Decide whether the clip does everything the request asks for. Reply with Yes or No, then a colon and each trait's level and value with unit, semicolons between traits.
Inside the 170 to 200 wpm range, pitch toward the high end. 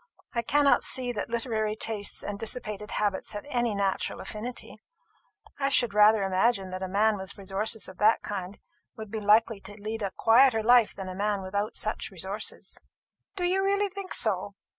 Yes: average, 180 wpm; high, 215 Hz